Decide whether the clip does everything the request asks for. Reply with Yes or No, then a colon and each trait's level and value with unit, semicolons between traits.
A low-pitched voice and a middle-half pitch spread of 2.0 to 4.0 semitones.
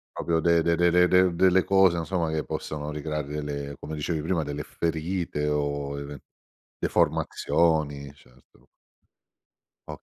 Yes: very low, 80 Hz; average, 2.8 semitones